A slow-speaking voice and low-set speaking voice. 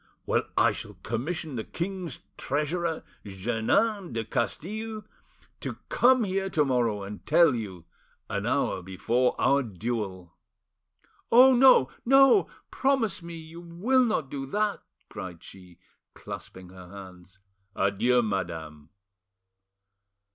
Yes: slow, 120 wpm; low, 130 Hz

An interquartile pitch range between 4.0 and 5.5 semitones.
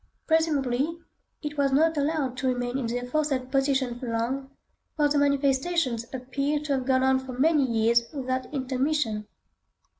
No: narrow, 2.6 semitones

